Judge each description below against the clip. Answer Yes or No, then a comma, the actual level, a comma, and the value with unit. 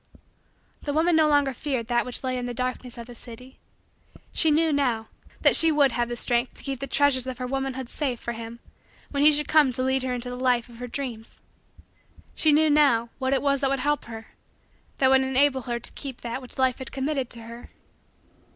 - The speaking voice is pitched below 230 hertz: No, very high, 260 Hz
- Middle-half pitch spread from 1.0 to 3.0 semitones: Yes, average, 2.7 semitones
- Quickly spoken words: Yes, fast, 215 wpm